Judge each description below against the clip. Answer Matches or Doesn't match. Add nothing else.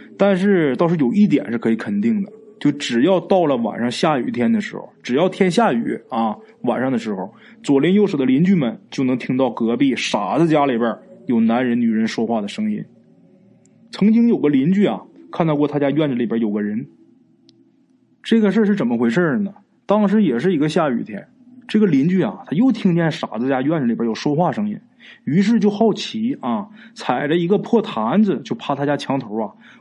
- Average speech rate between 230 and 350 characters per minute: Matches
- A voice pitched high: Matches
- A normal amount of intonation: Doesn't match